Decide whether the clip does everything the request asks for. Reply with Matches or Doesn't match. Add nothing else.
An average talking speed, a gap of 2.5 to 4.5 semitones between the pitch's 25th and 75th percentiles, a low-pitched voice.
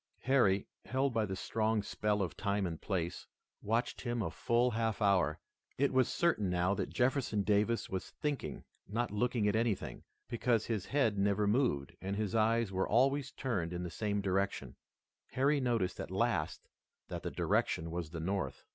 Matches